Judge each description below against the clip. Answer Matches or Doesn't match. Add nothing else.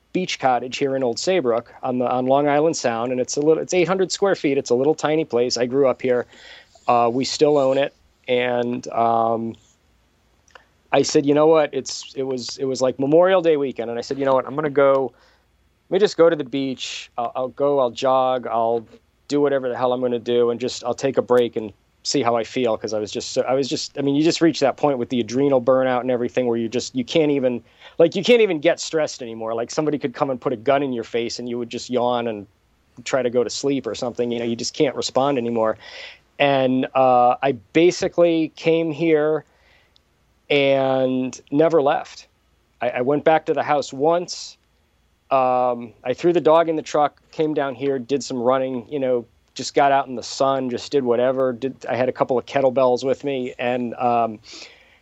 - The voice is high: Doesn't match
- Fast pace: Matches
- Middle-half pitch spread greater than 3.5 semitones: Doesn't match